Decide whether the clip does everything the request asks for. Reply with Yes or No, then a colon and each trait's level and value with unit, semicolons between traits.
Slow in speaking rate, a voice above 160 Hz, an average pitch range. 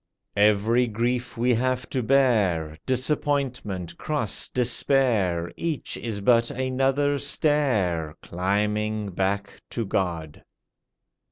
No: slow, 95 wpm; low, 115 Hz; average, 4.9 semitones